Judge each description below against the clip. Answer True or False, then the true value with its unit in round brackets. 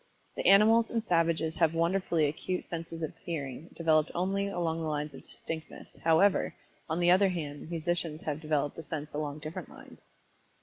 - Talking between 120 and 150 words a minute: False (170 wpm)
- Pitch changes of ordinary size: False (2.3 semitones)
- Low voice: False (165 Hz)